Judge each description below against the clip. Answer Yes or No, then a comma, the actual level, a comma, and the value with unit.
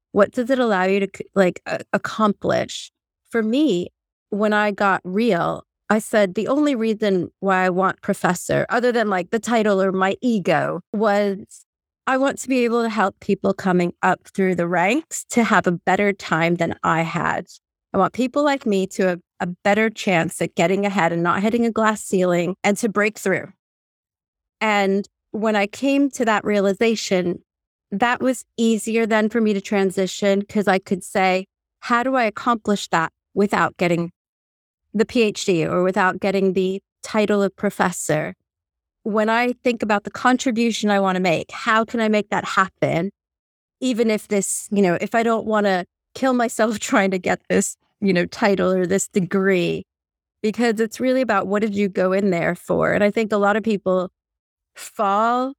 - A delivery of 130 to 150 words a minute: No, average, 180 wpm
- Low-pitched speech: No, high, 205 Hz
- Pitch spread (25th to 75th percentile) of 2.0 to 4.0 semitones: Yes, average, 3.2 semitones